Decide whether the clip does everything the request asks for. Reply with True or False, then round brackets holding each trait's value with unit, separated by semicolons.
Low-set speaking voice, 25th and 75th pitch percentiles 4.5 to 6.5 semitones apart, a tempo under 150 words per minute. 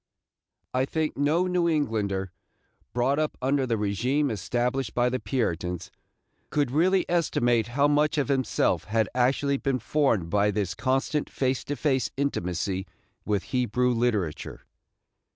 True (125 Hz; 5.0 semitones; 135 wpm)